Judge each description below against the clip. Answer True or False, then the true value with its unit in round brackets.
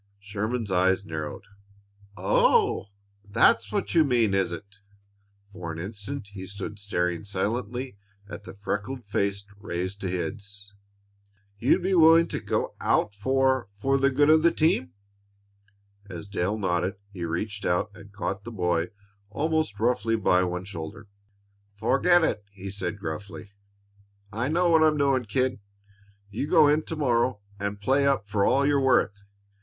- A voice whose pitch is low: True (105 Hz)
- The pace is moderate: True (150 wpm)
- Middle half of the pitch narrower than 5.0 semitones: False (5.3 semitones)